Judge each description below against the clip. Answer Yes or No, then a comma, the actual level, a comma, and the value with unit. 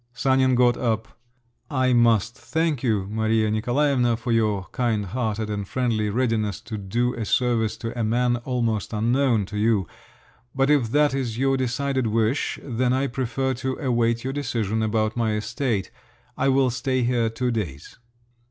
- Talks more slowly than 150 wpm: No, average, 155 wpm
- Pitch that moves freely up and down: No, average, 2.9 semitones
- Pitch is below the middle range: Yes, low, 120 Hz